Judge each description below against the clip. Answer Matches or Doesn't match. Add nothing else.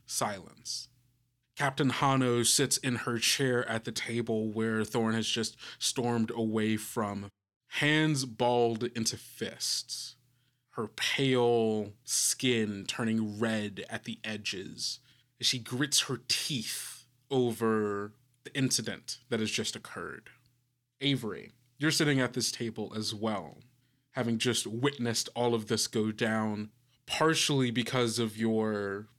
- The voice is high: Doesn't match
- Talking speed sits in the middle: Doesn't match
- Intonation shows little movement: Matches